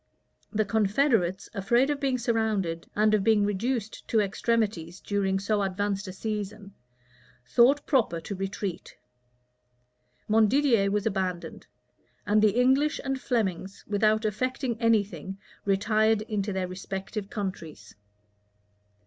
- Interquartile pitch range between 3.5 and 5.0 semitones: No, average, 2.9 semitones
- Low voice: No, high, 210 Hz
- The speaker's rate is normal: No, slow, 120 wpm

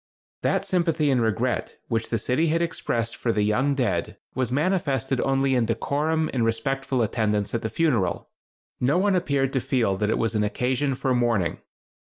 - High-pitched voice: No, low, 125 Hz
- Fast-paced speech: No, average, 175 wpm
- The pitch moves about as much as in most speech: Yes, average, 3.8 semitones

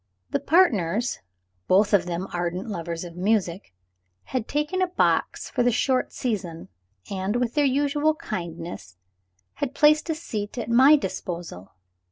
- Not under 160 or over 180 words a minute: No, average, 145 wpm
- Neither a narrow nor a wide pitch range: No, wide, 8.1 semitones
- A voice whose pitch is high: Yes, high, 215 Hz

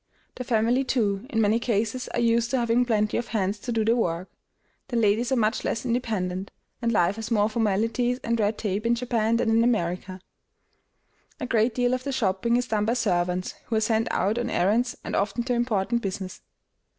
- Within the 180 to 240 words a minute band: Yes, average, 200 wpm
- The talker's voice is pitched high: Yes, high, 225 Hz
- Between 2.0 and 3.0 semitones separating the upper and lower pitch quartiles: Yes, average, 2.7 semitones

